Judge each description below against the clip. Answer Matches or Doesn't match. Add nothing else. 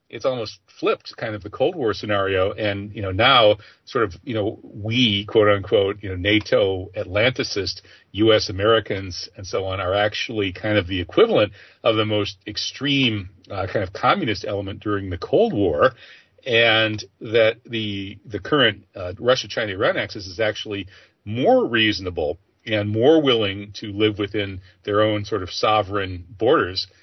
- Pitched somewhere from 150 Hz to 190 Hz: Doesn't match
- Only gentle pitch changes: Matches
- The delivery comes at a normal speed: Matches